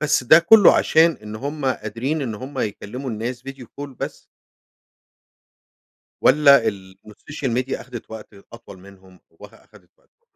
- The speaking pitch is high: No, low, 130 Hz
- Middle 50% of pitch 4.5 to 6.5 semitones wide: Yes, average, 5.1 semitones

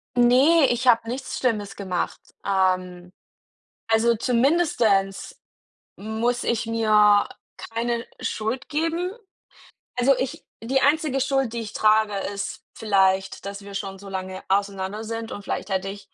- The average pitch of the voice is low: No, high, 220 Hz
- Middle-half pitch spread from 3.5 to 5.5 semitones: Yes, average, 4.0 semitones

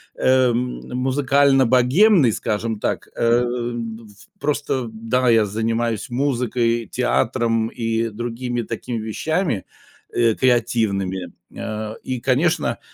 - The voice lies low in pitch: Yes, low, 120 Hz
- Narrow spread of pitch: Yes, narrow, 2.2 semitones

